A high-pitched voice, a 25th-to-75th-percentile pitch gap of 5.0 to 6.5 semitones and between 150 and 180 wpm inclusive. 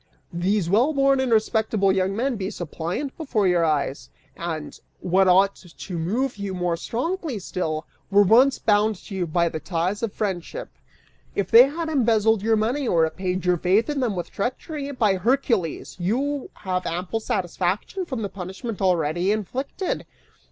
Yes: high, 200 Hz; average, 5.3 semitones; average, 165 wpm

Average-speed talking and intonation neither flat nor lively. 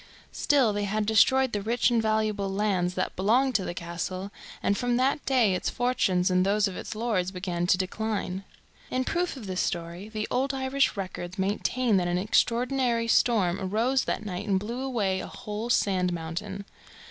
Yes: average, 180 wpm; average, 4.4 semitones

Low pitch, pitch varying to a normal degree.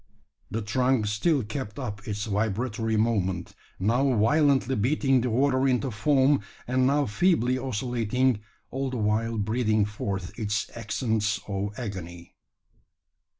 Yes: low, 115 Hz; average, 3.8 semitones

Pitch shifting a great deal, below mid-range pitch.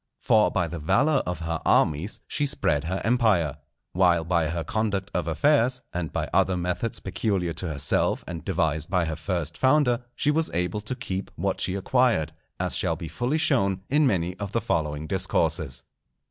Yes: wide, 5.7 semitones; very low, 90 Hz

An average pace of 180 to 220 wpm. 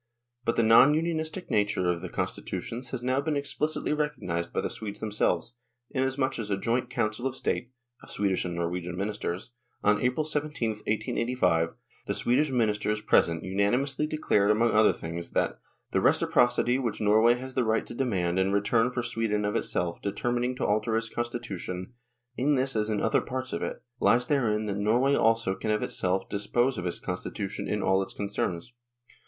Yes: average, 185 wpm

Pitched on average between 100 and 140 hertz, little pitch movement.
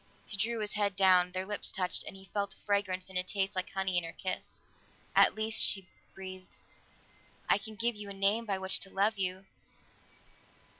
No: high, 195 Hz; narrow, 1.7 semitones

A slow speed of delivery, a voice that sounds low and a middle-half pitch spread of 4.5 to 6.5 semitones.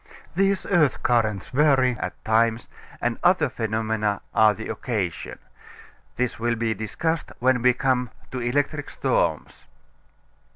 No: slow, 125 wpm; low, 120 Hz; average, 3.7 semitones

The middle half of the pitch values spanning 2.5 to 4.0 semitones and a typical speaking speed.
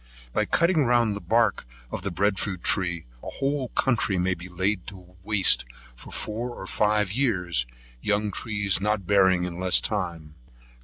Yes: average, 3.1 semitones; average, 160 wpm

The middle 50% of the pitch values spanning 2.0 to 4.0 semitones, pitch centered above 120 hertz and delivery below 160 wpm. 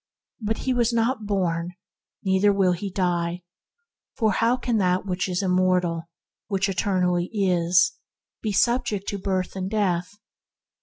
Yes: narrow, 2.6 semitones; high, 190 Hz; average, 140 wpm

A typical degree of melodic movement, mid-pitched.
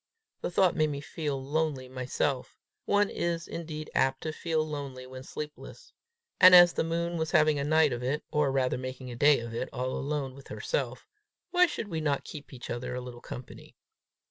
Yes: average, 3.7 semitones; medium, 145 Hz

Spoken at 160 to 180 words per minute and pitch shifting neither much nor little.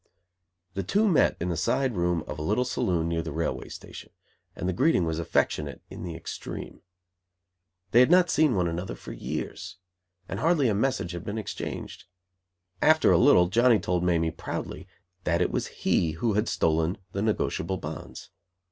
No: average, 175 wpm; wide, 6.2 semitones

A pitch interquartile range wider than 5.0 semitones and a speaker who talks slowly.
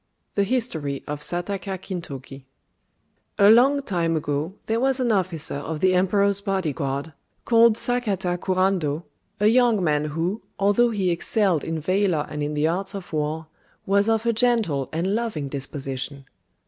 No: wide, 5.6 semitones; average, 160 wpm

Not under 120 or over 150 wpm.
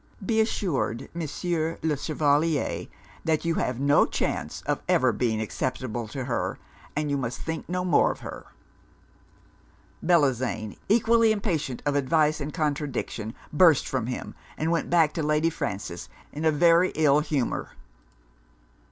Yes: average, 145 wpm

